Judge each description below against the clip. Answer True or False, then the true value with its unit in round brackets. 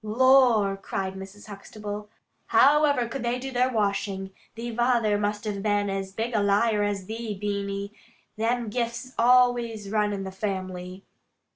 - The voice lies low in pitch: False (210 Hz)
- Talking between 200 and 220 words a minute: False (155 wpm)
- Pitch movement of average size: True (3.1 semitones)